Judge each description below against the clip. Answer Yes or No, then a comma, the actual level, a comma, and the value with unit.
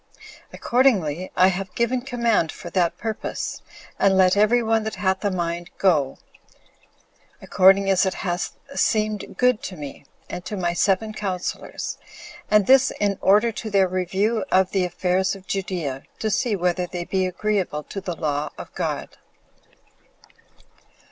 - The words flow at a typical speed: Yes, average, 150 wpm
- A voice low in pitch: No, high, 190 Hz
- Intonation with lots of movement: No, average, 3.0 semitones